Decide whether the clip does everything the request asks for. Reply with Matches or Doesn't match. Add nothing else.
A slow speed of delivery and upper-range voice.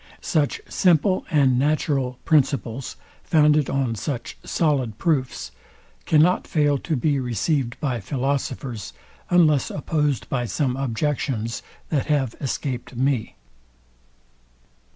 Doesn't match